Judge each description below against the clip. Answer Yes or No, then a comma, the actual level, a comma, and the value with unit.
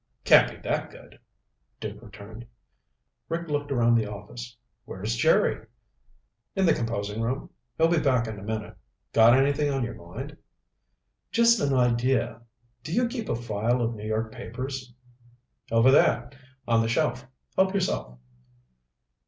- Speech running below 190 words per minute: Yes, average, 145 wpm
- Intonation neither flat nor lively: Yes, average, 3.9 semitones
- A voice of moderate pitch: No, low, 120 Hz